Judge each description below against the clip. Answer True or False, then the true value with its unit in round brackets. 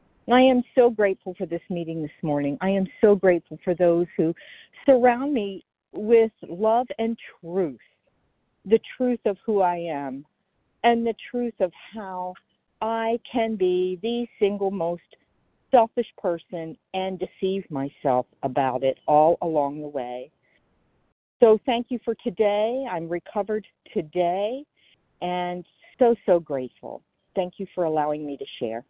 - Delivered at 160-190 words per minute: False (145 wpm)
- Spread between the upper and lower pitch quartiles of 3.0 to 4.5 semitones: False (5.2 semitones)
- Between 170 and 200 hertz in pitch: True (190 Hz)